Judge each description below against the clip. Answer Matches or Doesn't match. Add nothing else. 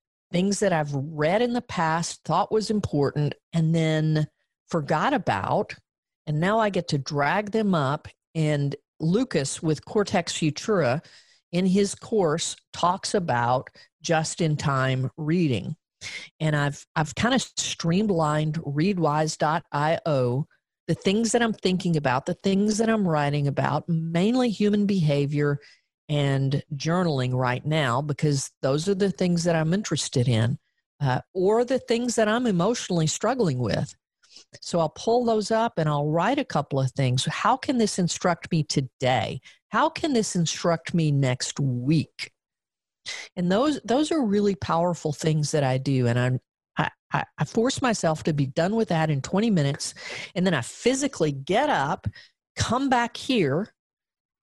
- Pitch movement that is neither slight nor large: Doesn't match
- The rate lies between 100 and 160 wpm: Matches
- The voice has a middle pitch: Matches